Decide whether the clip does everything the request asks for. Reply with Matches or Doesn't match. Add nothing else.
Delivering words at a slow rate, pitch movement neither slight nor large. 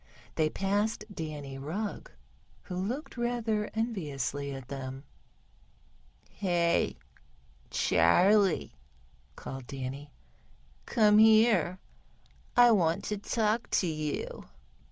Doesn't match